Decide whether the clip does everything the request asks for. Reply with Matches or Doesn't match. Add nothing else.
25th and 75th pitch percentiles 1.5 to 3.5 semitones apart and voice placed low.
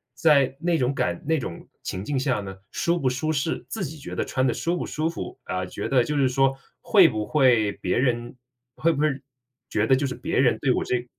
Doesn't match